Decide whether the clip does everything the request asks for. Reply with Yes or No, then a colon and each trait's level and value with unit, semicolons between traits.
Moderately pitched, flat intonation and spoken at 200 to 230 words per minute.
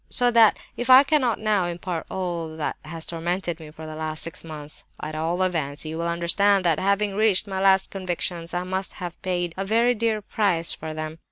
No: medium, 175 Hz; average, 3.5 semitones; fast, 205 wpm